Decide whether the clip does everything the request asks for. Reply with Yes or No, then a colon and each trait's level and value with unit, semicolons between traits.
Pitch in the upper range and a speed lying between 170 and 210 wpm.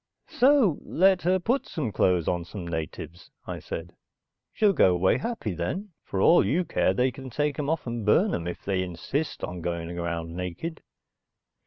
No: low, 105 Hz; average, 185 wpm